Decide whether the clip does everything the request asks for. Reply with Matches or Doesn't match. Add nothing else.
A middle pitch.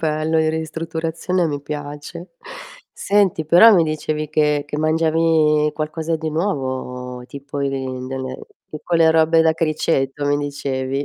Matches